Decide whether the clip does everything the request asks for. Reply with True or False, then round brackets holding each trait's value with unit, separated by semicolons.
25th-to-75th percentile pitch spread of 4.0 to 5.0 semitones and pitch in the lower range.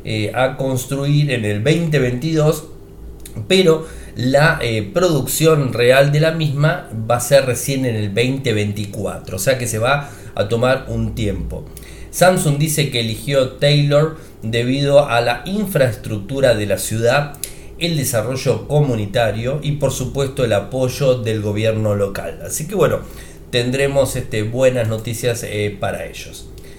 True (4.7 semitones; 125 Hz)